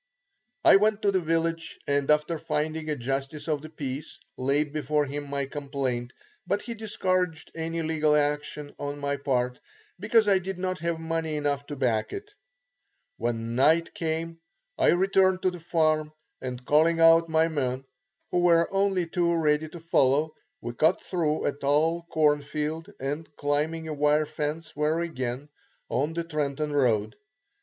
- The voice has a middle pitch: Yes, medium, 155 Hz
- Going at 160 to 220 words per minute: Yes, average, 165 wpm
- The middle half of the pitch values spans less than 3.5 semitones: Yes, average, 2.7 semitones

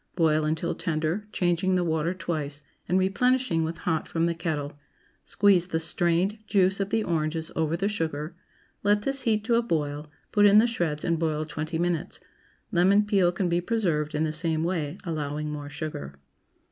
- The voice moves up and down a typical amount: Yes, average, 3.7 semitones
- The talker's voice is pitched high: No, medium, 170 Hz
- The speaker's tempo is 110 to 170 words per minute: No, average, 180 wpm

